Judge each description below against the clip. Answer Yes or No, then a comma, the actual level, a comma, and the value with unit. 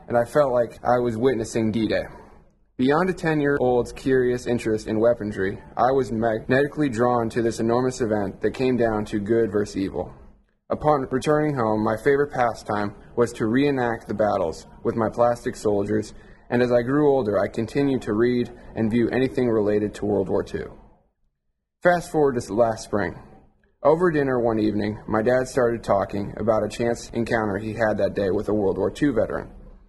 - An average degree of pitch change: Yes, average, 3.0 semitones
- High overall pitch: No, low, 115 Hz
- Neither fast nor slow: Yes, average, 185 wpm